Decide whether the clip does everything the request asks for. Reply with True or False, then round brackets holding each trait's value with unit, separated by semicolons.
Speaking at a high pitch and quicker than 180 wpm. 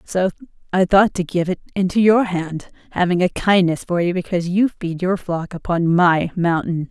False (180 Hz; 190 wpm)